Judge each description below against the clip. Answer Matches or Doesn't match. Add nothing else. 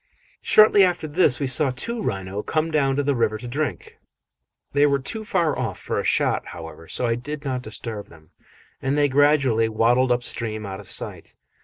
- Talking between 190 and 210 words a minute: Matches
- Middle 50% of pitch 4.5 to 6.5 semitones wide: Matches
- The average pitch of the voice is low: Matches